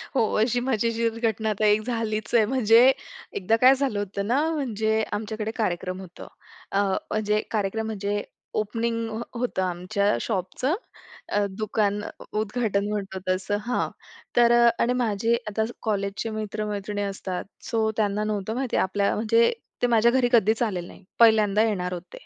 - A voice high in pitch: Yes, high, 215 Hz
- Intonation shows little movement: Yes, narrow, 2.2 semitones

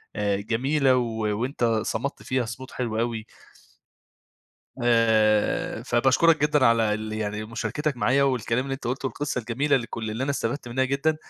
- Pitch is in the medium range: No, low, 120 Hz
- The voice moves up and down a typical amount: Yes, average, 3.3 semitones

